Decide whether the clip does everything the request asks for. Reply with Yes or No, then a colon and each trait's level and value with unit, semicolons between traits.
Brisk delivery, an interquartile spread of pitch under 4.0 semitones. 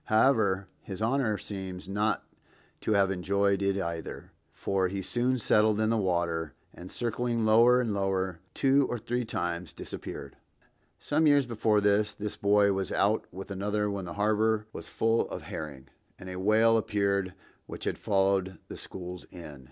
No: average, 165 wpm; average, 2.8 semitones